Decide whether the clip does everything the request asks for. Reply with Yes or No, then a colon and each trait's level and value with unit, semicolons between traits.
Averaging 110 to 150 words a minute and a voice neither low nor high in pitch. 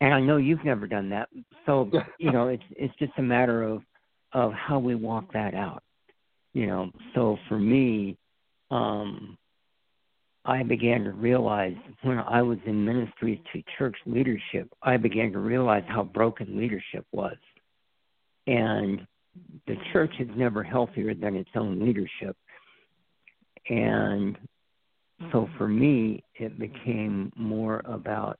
No: average, 140 wpm; low, 115 Hz